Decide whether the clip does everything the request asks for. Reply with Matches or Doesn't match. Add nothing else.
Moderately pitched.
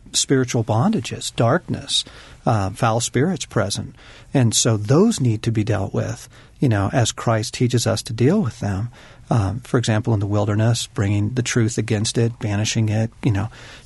Doesn't match